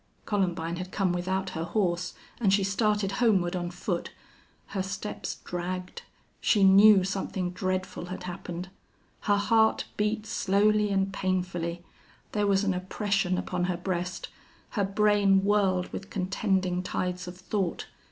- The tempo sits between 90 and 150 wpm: Yes, average, 140 wpm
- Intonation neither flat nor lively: No, narrow, 2.0 semitones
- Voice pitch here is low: No, high, 190 Hz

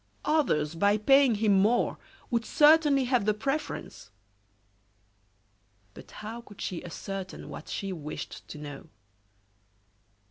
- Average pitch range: No, wide, 6.1 semitones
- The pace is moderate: No, slow, 115 wpm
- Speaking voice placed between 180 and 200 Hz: No, high, 215 Hz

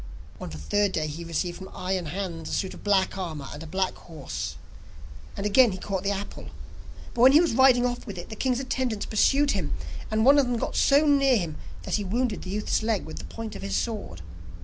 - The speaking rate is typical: No, fast, 235 wpm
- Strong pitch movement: Yes, wide, 5.8 semitones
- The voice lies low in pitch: No, high, 205 Hz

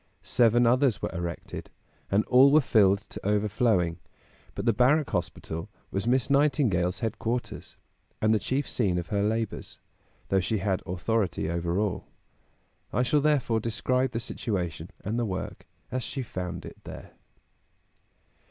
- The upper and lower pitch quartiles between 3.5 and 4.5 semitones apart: No, average, 4.9 semitones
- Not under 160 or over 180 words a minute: No, average, 145 wpm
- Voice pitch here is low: Yes, low, 110 Hz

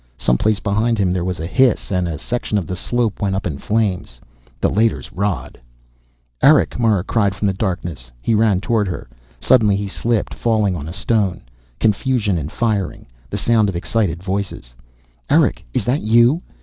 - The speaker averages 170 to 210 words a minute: Yes, average, 175 wpm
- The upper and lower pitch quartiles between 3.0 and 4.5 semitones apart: Yes, average, 3.7 semitones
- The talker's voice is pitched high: No, low, 100 Hz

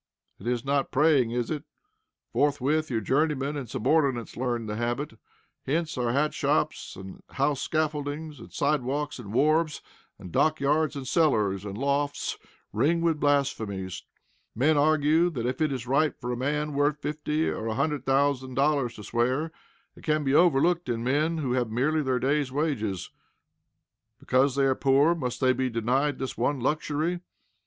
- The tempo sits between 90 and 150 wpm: No, average, 165 wpm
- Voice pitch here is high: No, medium, 140 Hz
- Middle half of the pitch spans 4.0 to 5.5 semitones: No, average, 3.4 semitones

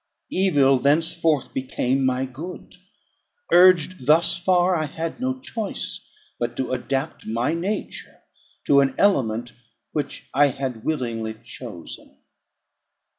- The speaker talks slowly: Yes, slow, 115 wpm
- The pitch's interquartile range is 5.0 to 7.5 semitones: Yes, average, 5.3 semitones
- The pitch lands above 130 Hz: Yes, medium, 140 Hz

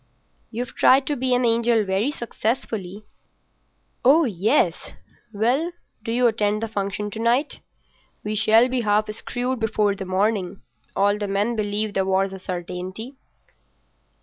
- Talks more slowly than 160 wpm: Yes, average, 145 wpm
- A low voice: No, high, 215 Hz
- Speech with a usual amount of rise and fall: Yes, average, 3.1 semitones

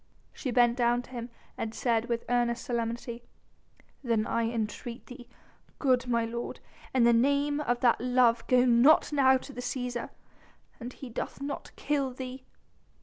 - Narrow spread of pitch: Yes, narrow, 1.7 semitones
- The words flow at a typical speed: Yes, average, 160 wpm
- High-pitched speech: Yes, high, 245 Hz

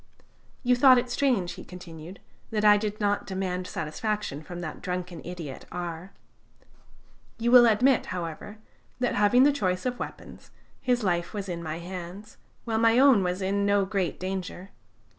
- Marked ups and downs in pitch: No, average, 4.0 semitones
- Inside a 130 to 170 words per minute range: Yes, average, 160 wpm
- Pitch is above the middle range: Yes, high, 195 Hz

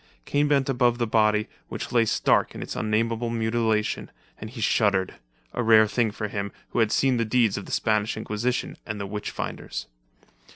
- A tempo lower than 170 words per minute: No, average, 190 wpm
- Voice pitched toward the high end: No, low, 110 Hz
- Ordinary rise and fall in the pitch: No, narrow, 2.0 semitones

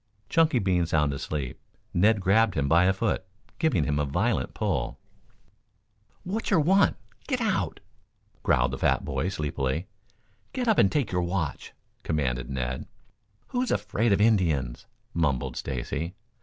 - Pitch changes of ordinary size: No, wide, 7.7 semitones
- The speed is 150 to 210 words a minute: No, average, 140 wpm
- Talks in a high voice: No, very low, 90 Hz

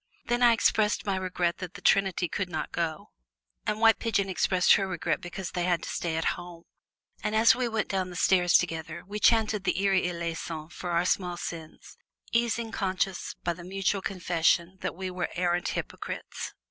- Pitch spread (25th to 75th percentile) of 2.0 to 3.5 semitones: Yes, narrow, 2.5 semitones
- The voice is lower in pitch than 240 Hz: Yes, medium, 185 Hz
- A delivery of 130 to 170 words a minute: No, average, 185 wpm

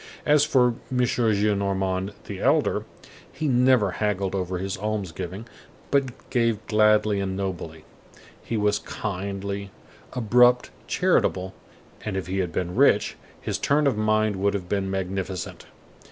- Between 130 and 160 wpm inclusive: Yes, average, 140 wpm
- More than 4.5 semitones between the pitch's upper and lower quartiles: No, average, 3.3 semitones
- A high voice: No, low, 100 Hz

